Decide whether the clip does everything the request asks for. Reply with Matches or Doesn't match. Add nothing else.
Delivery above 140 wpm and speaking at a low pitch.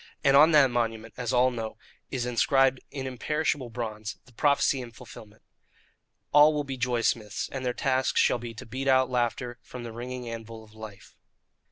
Matches